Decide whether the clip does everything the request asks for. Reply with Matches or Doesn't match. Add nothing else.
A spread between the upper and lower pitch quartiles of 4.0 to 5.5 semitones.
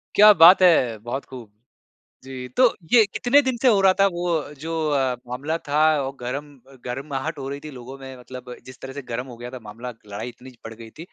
Matches